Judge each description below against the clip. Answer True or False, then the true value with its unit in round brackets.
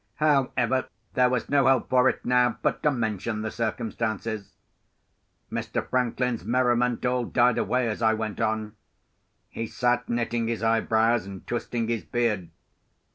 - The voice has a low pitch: True (120 Hz)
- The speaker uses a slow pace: False (145 wpm)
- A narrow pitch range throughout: True (2.0 semitones)